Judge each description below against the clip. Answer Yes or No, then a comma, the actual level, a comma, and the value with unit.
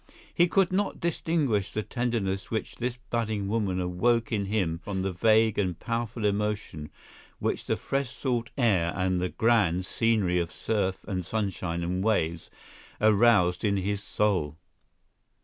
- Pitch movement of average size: Yes, average, 4.0 semitones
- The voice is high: No, low, 105 Hz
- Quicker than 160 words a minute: No, average, 150 wpm